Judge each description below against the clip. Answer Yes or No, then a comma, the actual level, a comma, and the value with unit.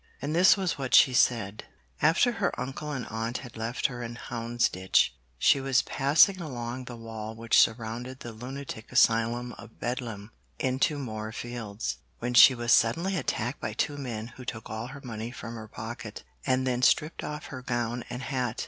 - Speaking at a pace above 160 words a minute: Yes, average, 175 wpm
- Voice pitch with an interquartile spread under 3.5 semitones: Yes, average, 2.8 semitones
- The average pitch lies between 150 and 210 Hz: No, low, 120 Hz